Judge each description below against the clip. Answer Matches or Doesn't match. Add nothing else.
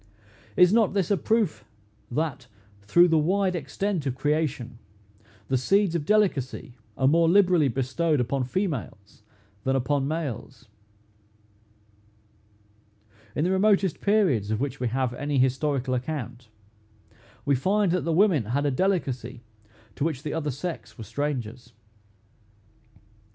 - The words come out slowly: Matches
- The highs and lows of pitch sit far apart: Matches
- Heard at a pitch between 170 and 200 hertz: Doesn't match